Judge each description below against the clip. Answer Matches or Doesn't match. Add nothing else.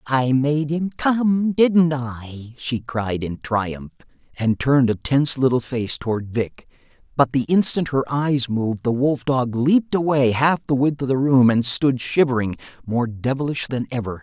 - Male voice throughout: Matches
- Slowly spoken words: Doesn't match